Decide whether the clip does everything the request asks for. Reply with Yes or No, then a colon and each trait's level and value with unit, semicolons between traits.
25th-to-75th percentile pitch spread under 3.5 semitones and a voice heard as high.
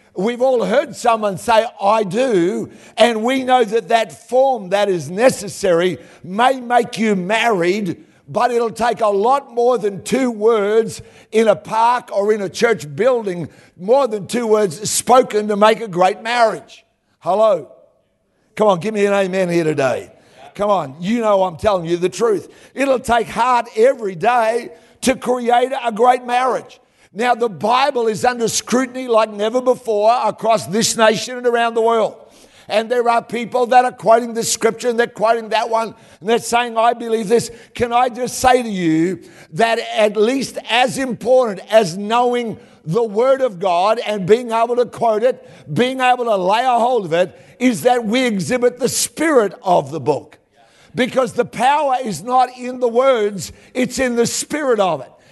Yes: average, 3.0 semitones; high, 230 Hz